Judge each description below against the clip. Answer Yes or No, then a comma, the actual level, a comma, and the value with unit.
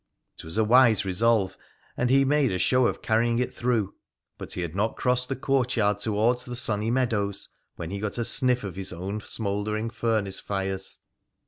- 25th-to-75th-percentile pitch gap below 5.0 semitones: Yes, average, 3.7 semitones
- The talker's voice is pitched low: Yes, low, 110 Hz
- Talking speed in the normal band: Yes, average, 190 wpm